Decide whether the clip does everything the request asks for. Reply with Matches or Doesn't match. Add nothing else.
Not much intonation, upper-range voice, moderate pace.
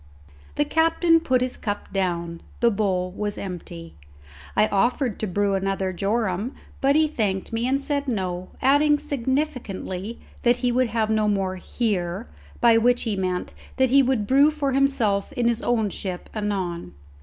Doesn't match